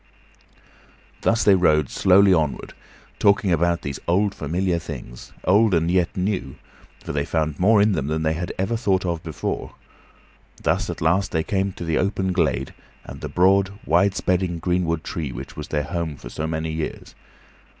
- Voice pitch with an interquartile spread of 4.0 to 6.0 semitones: No, average, 3.4 semitones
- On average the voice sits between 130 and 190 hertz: No, very low, 85 Hz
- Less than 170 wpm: No, average, 175 wpm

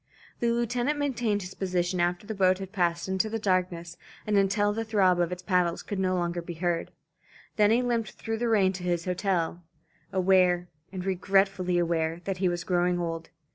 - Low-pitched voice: No, medium, 185 Hz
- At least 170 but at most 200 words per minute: Yes, average, 190 wpm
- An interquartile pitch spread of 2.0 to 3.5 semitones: Yes, average, 2.7 semitones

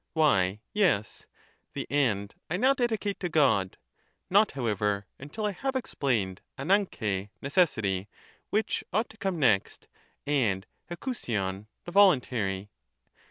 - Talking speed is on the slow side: Yes, slow, 120 wpm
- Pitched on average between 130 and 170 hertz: Yes, medium, 140 Hz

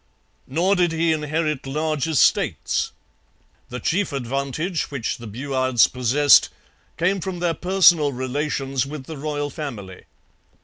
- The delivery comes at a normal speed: No, slow, 125 wpm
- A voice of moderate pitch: Yes, medium, 145 Hz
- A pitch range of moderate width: Yes, average, 3.8 semitones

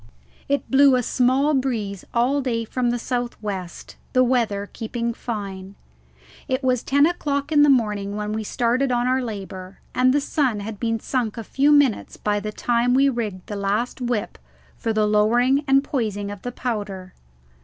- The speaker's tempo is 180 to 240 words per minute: Yes, average, 185 wpm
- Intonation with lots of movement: No, average, 3.7 semitones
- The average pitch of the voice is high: Yes, high, 235 Hz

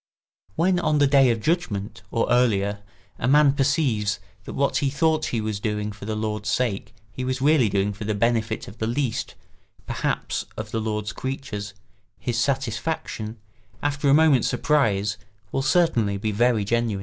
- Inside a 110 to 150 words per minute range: No, average, 170 wpm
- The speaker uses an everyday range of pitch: Yes, average, 4.7 semitones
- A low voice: Yes, low, 115 Hz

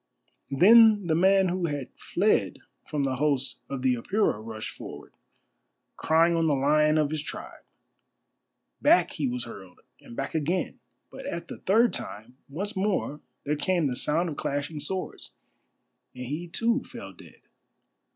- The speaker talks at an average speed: Yes, average, 155 wpm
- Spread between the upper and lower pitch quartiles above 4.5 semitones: Yes, average, 5.3 semitones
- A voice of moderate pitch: Yes, medium, 155 Hz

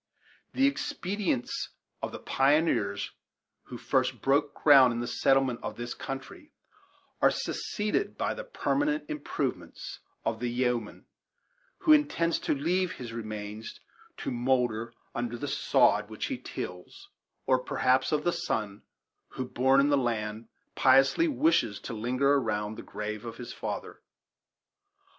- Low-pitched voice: Yes, low, 130 Hz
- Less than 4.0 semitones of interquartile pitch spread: No, average, 4.7 semitones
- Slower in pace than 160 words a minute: Yes, average, 140 wpm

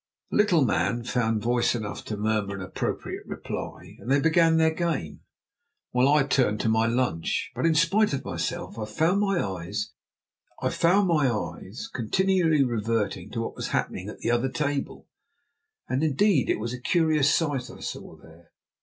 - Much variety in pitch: Yes, wide, 6.8 semitones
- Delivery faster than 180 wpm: No, average, 165 wpm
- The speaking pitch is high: No, low, 130 Hz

